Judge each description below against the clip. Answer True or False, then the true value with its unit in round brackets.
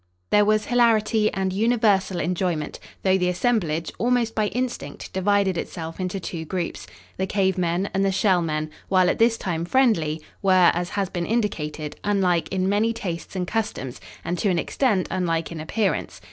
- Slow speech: False (175 wpm)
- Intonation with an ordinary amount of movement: True (3.7 semitones)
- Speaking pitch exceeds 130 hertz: True (190 Hz)